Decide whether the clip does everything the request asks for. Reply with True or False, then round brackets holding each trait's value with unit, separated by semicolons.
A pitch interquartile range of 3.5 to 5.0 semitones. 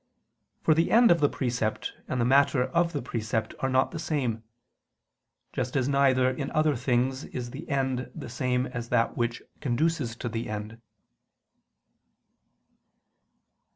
False (3.0 semitones)